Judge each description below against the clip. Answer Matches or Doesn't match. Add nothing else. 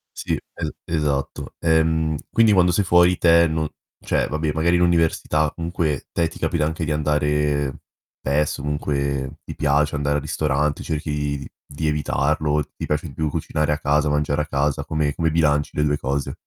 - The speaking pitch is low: Matches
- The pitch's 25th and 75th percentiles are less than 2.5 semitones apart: Matches